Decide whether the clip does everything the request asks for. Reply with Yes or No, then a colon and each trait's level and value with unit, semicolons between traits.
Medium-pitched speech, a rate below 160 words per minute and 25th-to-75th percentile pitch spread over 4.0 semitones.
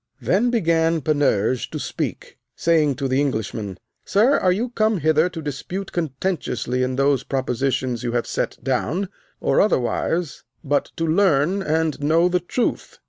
Yes: medium, 155 Hz; average, 150 wpm; wide, 5.4 semitones